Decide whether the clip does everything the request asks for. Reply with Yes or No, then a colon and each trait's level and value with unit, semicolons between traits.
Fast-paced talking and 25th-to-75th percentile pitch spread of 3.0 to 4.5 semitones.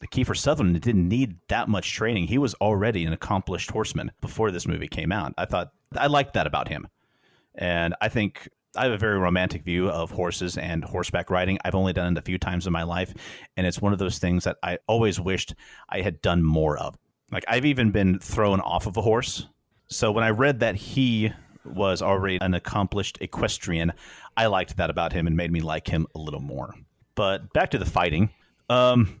Yes: fast, 215 wpm; average, 3.9 semitones